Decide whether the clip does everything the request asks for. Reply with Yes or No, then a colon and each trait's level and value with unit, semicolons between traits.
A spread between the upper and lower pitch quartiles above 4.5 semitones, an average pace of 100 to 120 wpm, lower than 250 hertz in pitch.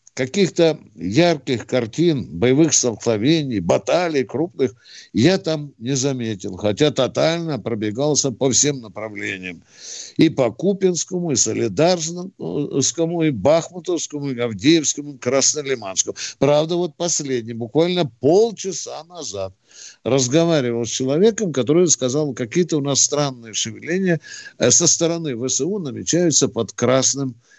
Yes: average, 5.2 semitones; slow, 110 wpm; medium, 140 Hz